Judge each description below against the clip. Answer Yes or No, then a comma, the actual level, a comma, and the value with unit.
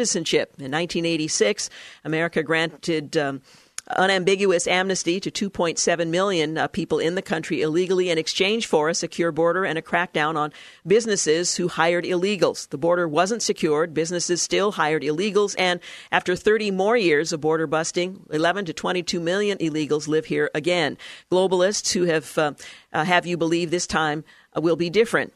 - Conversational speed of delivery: Yes, average, 160 wpm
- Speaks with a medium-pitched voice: Yes, medium, 170 Hz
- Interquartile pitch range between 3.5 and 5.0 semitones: No, average, 2.7 semitones